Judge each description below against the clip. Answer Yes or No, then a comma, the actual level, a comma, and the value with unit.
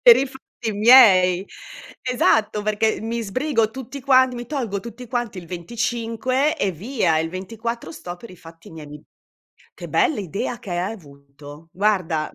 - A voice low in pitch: No, high, 215 Hz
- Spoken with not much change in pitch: No, wide, 5.5 semitones